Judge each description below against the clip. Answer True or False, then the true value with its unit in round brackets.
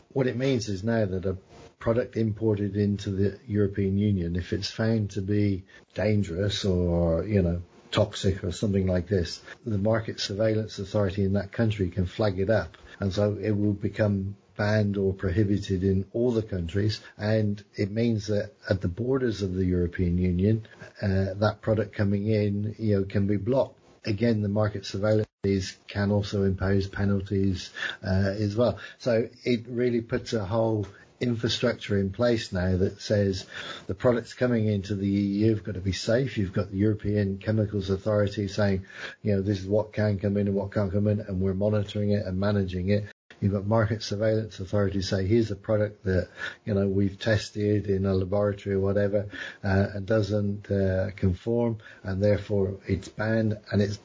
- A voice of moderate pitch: False (105 Hz)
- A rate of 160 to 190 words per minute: True (180 wpm)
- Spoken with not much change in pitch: True (1.8 semitones)